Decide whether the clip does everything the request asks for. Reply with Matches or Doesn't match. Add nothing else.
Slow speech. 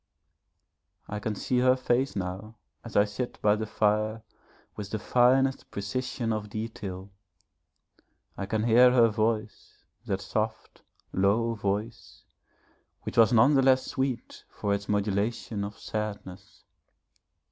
Matches